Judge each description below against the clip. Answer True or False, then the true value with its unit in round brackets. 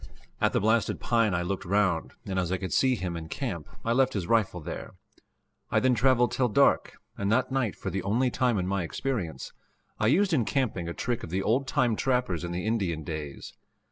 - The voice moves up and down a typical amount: False (5.8 semitones)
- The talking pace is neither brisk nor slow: False (215 wpm)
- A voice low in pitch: True (105 Hz)